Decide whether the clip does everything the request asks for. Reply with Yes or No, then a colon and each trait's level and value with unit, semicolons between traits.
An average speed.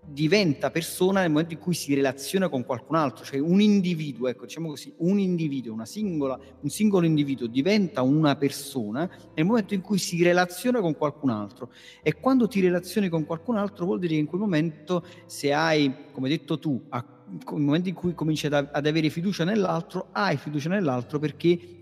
No: fast, 190 wpm